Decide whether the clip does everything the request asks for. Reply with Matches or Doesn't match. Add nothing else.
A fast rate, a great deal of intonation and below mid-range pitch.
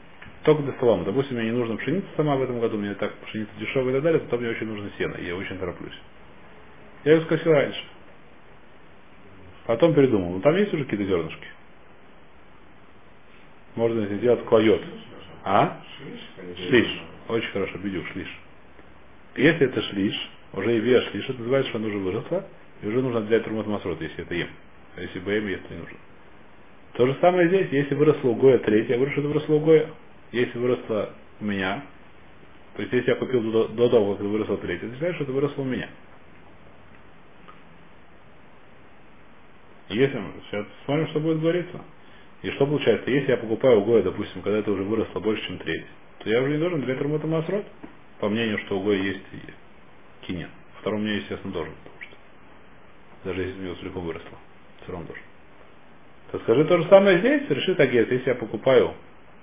Matches